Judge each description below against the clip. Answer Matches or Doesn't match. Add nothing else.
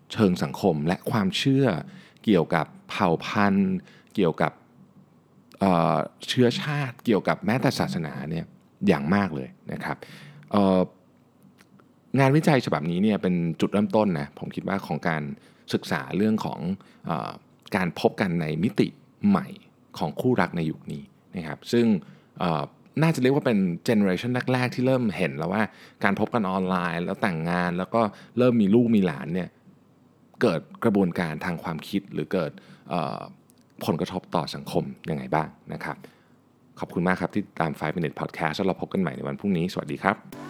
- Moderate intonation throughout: Doesn't match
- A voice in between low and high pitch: Doesn't match